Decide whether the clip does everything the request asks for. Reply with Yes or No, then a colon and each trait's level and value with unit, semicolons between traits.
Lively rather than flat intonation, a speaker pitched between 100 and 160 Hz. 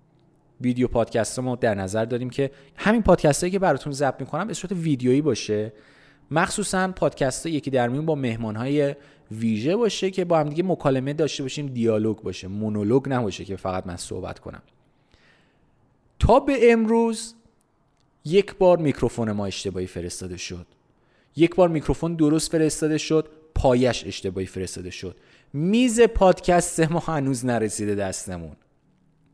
Yes: wide, 6.7 semitones; medium, 140 Hz